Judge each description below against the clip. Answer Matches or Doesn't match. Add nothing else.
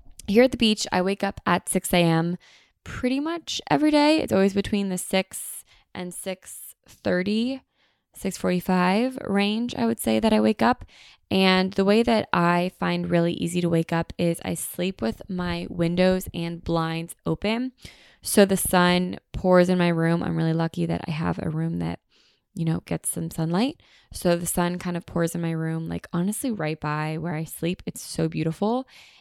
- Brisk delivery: Doesn't match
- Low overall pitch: Doesn't match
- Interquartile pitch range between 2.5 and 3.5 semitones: Matches